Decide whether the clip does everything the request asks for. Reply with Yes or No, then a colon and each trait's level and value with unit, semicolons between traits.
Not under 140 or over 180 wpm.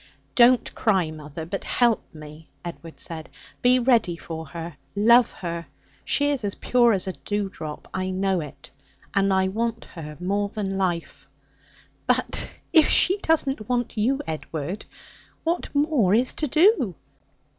Yes: average, 150 wpm